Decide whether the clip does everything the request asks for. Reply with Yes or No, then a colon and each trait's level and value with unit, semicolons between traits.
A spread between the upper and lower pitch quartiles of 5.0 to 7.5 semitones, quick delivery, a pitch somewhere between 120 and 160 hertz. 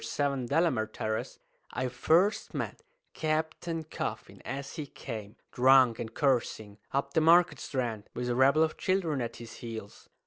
No: average, 5.3 semitones; average, 150 wpm; low, 135 Hz